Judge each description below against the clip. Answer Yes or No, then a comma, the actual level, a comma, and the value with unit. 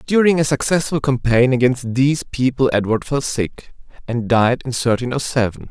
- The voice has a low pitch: Yes, low, 130 Hz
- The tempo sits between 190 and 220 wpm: No, average, 170 wpm